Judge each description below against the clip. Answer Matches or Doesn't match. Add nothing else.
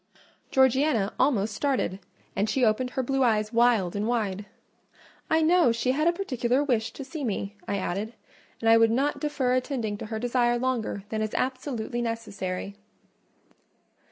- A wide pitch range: Doesn't match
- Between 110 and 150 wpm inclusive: Doesn't match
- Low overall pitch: Doesn't match